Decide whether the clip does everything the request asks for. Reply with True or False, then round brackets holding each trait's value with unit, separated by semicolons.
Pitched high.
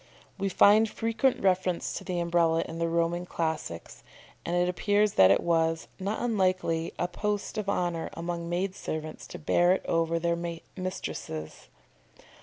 False (175 Hz)